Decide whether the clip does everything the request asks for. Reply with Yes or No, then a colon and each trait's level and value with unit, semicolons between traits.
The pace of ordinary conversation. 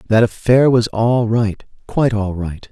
Yes: average, 175 wpm